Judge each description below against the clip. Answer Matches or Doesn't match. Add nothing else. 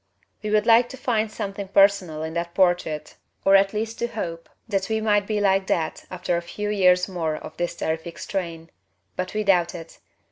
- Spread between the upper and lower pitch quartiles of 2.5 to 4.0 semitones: Matches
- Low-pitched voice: Doesn't match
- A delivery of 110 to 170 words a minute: Doesn't match